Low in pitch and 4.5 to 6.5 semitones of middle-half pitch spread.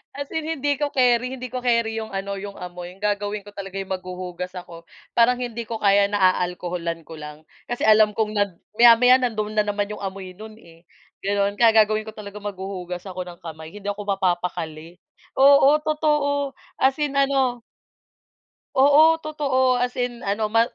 No: high, 210 Hz; average, 5.0 semitones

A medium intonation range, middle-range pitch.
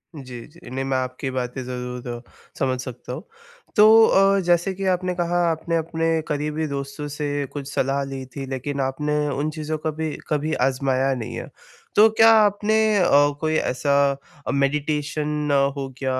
Yes: average, 3.6 semitones; medium, 150 Hz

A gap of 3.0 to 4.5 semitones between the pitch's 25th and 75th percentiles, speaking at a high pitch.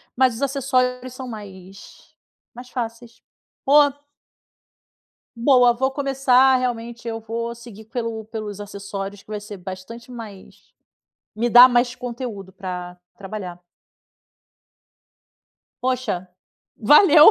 Yes: average, 3.6 semitones; high, 235 Hz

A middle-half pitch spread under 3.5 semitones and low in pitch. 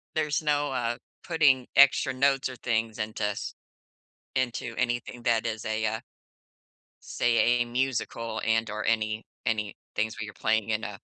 Yes: average, 2.8 semitones; low, 115 Hz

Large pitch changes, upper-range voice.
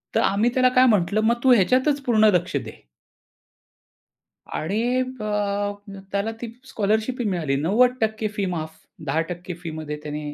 Yes: wide, 6.2 semitones; high, 205 Hz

